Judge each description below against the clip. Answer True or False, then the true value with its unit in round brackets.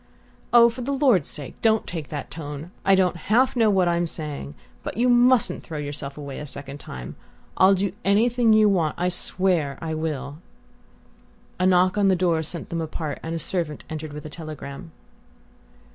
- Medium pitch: True (170 Hz)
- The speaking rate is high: False (180 wpm)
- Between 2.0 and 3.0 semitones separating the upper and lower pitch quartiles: False (4.9 semitones)